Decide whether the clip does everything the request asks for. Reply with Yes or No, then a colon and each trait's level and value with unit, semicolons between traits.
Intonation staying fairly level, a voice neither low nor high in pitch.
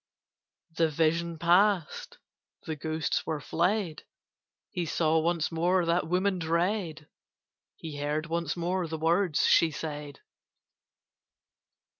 Yes: narrow, 1.9 semitones; medium, 165 Hz